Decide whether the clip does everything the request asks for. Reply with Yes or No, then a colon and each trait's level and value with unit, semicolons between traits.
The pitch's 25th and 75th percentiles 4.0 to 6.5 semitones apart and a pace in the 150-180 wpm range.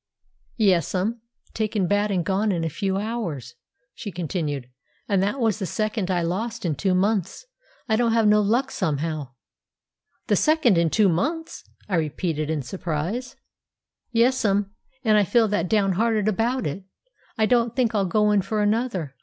Yes: average, 4.3 semitones; average, 160 wpm